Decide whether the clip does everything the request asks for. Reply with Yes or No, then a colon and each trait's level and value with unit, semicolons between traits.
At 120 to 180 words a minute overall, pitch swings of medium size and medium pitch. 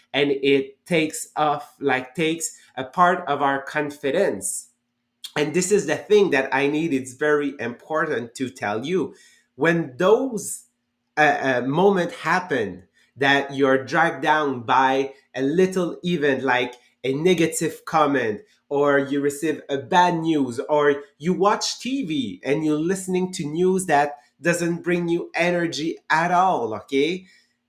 Yes: average, 145 wpm; average, 4.2 semitones; medium, 150 Hz